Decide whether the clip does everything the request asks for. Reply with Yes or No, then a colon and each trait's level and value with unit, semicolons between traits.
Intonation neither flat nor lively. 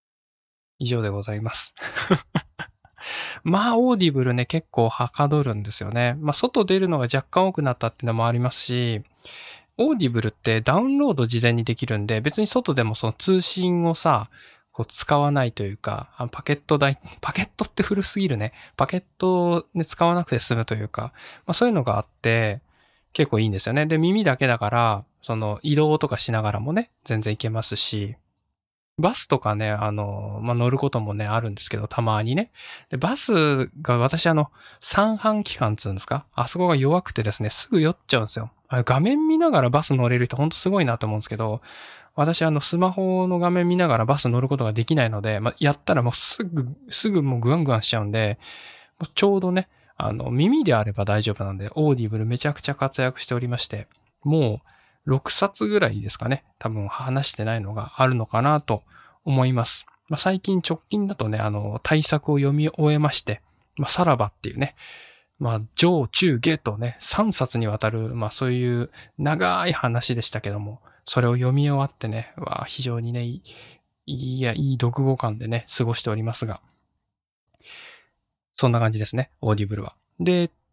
No: wide, 5.7 semitones